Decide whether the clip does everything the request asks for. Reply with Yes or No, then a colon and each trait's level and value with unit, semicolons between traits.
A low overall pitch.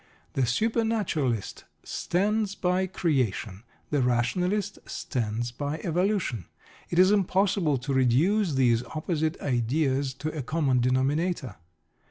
No: medium, 150 Hz